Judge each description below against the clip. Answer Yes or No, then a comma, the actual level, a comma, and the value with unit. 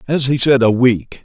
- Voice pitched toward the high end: No, low, 125 Hz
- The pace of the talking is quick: Yes, fast, 240 wpm